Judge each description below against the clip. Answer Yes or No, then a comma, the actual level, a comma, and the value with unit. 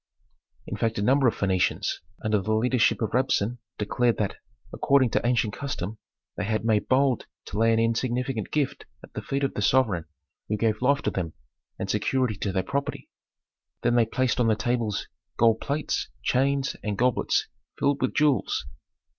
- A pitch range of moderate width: Yes, average, 3.6 semitones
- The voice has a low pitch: Yes, low, 115 Hz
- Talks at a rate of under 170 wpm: No, average, 175 wpm